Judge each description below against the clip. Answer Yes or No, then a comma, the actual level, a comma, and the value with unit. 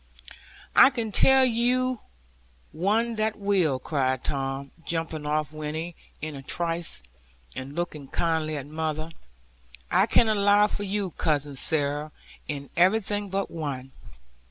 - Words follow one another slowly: Yes, slow, 130 wpm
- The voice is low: No, medium, 165 Hz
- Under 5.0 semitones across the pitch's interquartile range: No, wide, 5.6 semitones